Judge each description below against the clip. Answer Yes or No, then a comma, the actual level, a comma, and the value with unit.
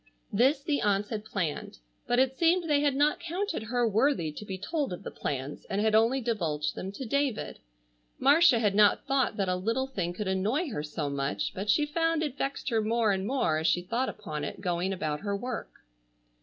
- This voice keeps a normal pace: No, fast, 210 wpm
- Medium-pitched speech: No, high, 220 Hz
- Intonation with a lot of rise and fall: Yes, wide, 6.6 semitones